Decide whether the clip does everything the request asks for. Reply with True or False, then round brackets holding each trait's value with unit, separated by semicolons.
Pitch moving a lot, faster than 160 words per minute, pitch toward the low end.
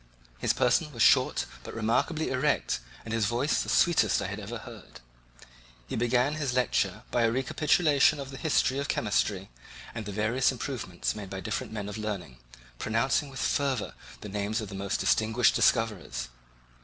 False (4.3 semitones; 170 wpm; 115 Hz)